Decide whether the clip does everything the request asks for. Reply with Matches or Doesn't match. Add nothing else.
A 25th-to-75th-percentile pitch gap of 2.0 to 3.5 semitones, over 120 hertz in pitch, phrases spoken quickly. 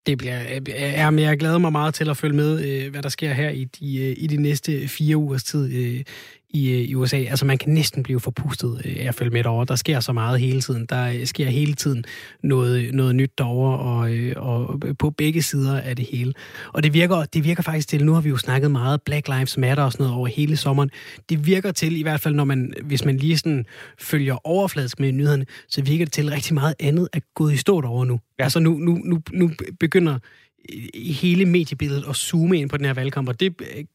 Matches